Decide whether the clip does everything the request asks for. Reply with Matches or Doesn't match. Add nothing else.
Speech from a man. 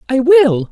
Matches